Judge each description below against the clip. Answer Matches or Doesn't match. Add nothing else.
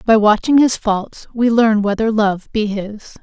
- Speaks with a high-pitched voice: Matches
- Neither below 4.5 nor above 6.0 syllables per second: Doesn't match